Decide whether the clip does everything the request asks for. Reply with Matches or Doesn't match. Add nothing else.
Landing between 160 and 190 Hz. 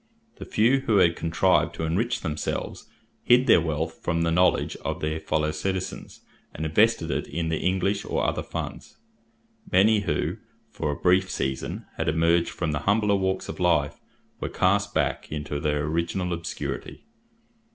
Doesn't match